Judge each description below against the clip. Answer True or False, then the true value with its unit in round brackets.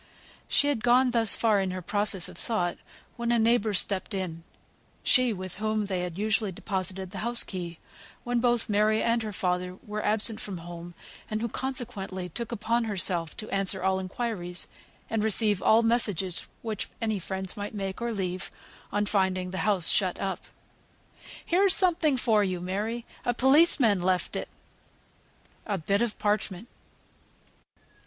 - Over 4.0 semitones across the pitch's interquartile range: False (3.7 semitones)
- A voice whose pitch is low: False (205 Hz)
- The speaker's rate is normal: True (160 wpm)